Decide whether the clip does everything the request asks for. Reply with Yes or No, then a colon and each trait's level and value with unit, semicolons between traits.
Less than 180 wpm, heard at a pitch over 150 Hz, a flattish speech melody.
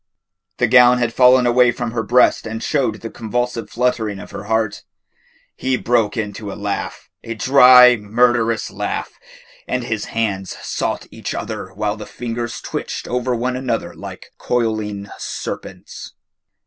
No: average, 150 wpm; low, 115 Hz; narrow, 2.3 semitones